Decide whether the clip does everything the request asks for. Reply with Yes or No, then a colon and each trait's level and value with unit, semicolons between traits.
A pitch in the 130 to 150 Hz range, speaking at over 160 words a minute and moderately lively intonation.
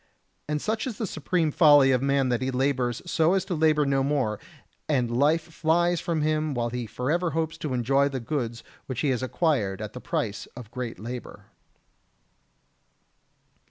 Yes: medium, 140 Hz; average, 175 wpm; average, 4.4 semitones